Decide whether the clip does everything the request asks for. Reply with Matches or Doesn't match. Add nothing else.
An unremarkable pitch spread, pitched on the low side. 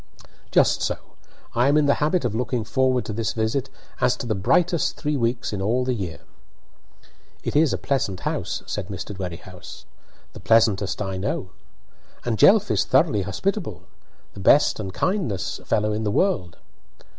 Doesn't match